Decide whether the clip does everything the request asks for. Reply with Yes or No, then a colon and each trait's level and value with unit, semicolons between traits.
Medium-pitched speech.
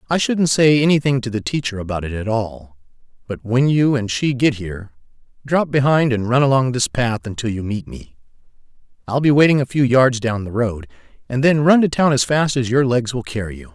No: low, 125 Hz